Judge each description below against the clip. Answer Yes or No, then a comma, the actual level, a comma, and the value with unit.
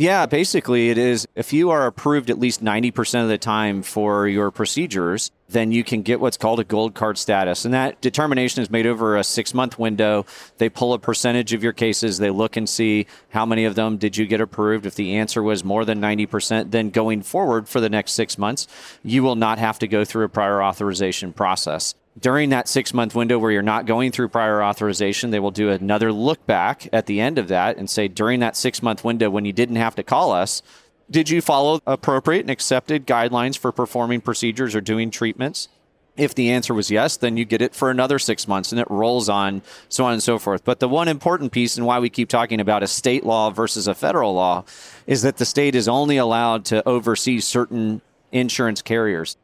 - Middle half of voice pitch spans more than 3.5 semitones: No, narrow, 2.6 semitones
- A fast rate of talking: Yes, fast, 225 wpm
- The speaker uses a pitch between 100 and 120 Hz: Yes, low, 115 Hz